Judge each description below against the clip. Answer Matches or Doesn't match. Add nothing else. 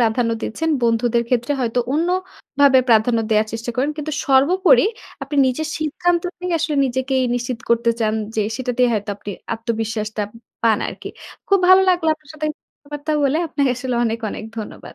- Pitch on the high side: Matches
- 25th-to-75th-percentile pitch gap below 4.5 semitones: Doesn't match